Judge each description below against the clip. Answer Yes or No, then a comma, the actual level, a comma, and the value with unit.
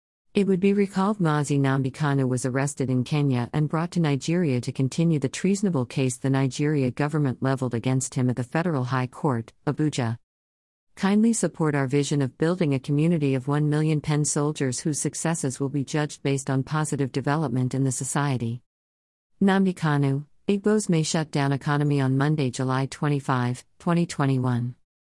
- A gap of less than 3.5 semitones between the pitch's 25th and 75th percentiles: Yes, average, 3.1 semitones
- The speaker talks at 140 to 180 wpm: Yes, average, 160 wpm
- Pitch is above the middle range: No, medium, 140 Hz